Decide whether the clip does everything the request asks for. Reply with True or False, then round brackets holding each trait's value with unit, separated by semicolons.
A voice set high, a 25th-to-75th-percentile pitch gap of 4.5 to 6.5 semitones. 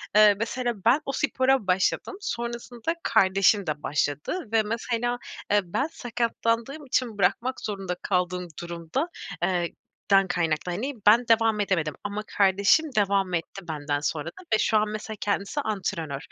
True (205 Hz; 4.8 semitones)